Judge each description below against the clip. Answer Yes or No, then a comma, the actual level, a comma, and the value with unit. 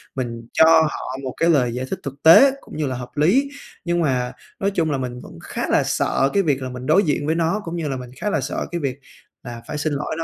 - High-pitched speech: No, medium, 145 Hz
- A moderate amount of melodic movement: Yes, average, 4.4 semitones